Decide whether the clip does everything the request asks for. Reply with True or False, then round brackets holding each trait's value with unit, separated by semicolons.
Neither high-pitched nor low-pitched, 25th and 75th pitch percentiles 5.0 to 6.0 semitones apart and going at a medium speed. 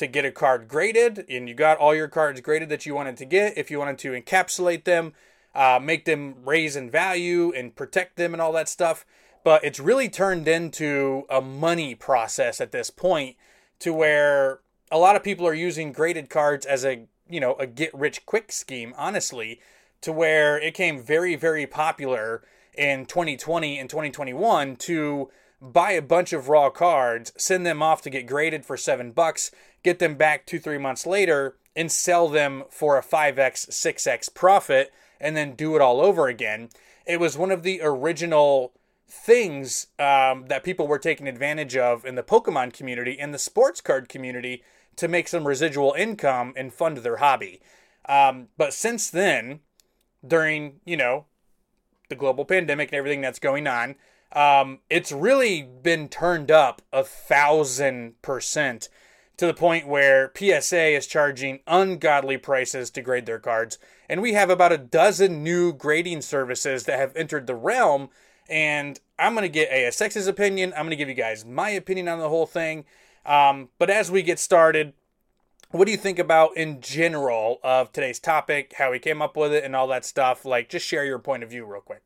False (150 Hz; 4.0 semitones; 185 wpm)